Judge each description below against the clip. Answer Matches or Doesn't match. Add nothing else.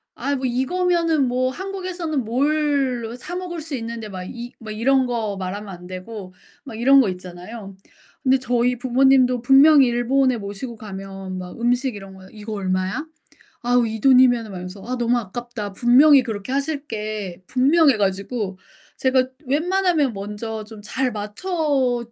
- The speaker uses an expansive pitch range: Doesn't match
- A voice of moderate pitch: Doesn't match